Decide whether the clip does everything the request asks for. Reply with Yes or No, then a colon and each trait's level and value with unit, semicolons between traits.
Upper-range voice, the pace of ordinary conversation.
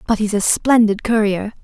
Yes: high, 215 Hz; average, 185 wpm